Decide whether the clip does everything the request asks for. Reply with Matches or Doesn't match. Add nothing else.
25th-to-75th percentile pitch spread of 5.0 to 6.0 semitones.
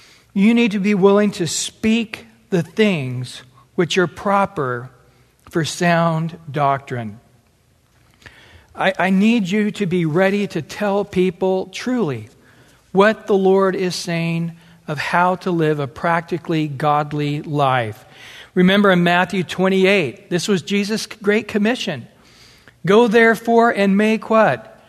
Matches